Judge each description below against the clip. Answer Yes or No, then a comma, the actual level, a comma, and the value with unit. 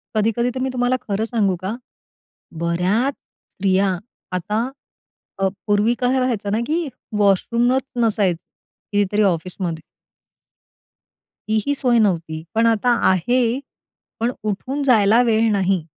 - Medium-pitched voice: No, high, 215 Hz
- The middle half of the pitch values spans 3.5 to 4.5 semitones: Yes, average, 3.9 semitones